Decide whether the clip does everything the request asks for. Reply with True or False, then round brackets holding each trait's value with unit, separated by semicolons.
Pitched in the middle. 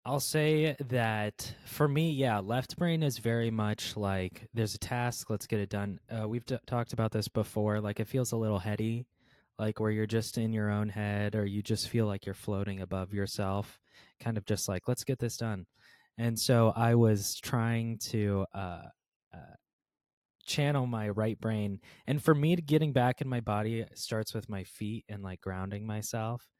False (110 Hz)